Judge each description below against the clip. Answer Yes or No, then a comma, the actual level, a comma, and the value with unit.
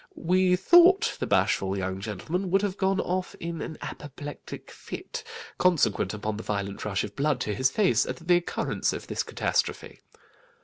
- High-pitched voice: No, medium, 150 Hz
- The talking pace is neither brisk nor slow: Yes, average, 170 wpm